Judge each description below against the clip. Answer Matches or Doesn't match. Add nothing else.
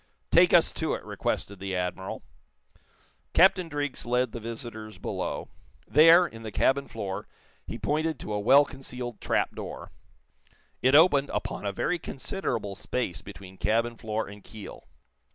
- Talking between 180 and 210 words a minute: Doesn't match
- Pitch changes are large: Matches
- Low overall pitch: Matches